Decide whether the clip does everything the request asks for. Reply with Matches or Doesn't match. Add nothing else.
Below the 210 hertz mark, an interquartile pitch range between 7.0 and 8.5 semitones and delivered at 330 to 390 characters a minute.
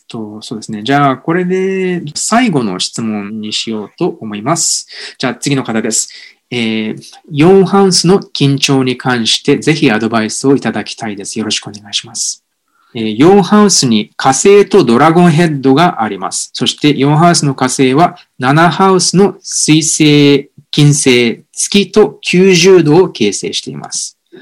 Doesn't match